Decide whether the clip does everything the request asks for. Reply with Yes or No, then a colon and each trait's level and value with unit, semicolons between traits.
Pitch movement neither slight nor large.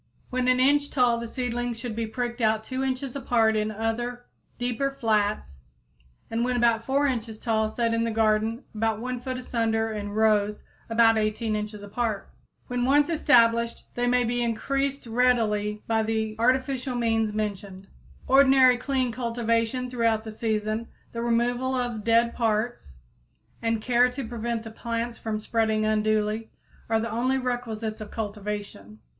No: narrow, 2.2 semitones